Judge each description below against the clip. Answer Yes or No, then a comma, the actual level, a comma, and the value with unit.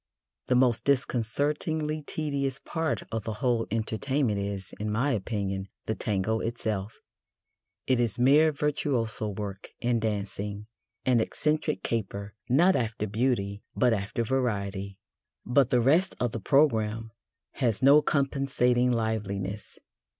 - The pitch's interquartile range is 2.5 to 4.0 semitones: No, average, 4.5 semitones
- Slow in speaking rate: Yes, slow, 125 wpm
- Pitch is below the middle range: Yes, low, 115 Hz